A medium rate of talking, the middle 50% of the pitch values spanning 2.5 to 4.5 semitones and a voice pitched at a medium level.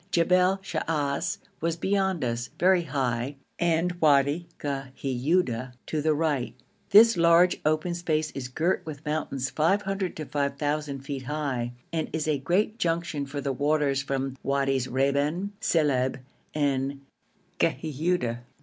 No: slow, 130 wpm; average, 3.7 semitones; medium, 150 Hz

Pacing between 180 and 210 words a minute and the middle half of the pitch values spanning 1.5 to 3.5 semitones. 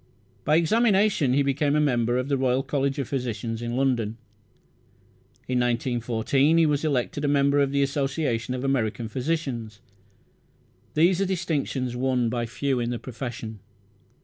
No: average, 150 wpm; average, 3.1 semitones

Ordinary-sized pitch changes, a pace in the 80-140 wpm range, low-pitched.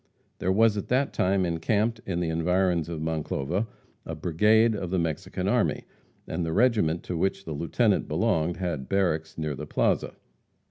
No: average, 3.5 semitones; average, 170 wpm; very low, 90 Hz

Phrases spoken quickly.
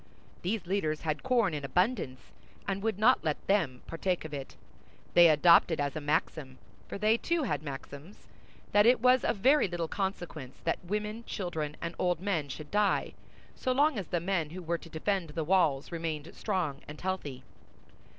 No: average, 170 wpm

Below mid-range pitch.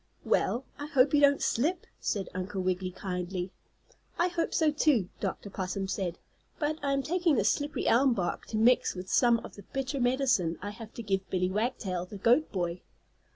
No: high, 220 Hz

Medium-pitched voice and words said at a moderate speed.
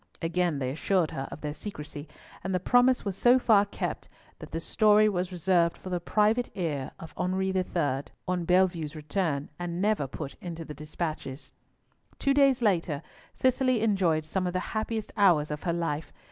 Yes: medium, 180 Hz; average, 175 wpm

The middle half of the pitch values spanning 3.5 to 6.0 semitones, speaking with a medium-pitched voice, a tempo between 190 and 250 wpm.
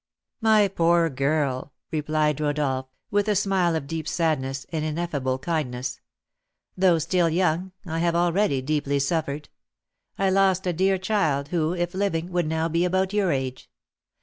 No: average, 3.9 semitones; medium, 165 Hz; average, 150 wpm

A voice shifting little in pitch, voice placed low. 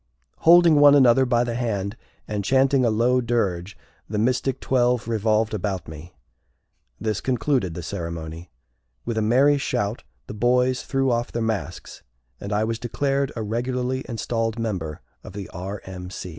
No: average, 3.9 semitones; low, 115 Hz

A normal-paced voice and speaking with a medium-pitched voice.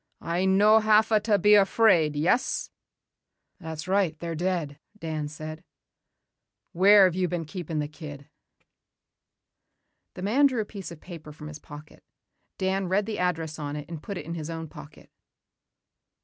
Yes: average, 160 wpm; medium, 170 Hz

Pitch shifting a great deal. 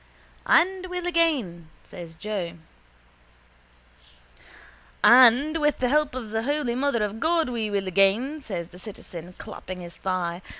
Yes: wide, 8.2 semitones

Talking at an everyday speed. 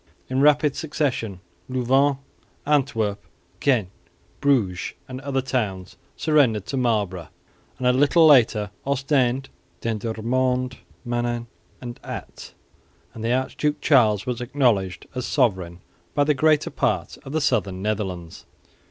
No: slow, 120 wpm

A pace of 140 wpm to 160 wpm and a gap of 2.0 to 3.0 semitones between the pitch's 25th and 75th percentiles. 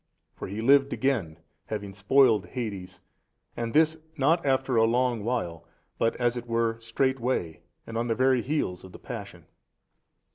No: average, 155 wpm; average, 3.7 semitones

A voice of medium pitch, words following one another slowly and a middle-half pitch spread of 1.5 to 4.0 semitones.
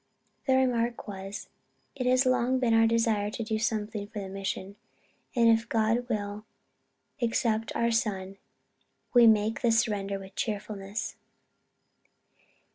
No: high, 220 Hz; slow, 130 wpm; narrow, 2.4 semitones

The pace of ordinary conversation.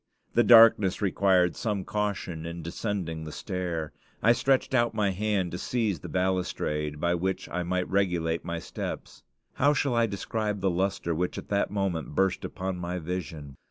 Yes: average, 170 wpm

